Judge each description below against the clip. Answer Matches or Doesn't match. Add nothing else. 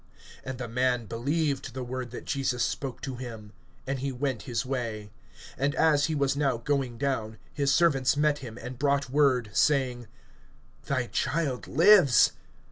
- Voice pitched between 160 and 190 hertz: Doesn't match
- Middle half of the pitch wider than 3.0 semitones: Doesn't match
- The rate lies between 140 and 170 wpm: Matches